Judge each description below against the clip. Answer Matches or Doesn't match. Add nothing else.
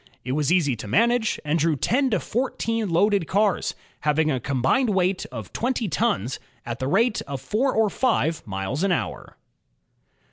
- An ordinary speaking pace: Matches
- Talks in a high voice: Doesn't match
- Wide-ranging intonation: Matches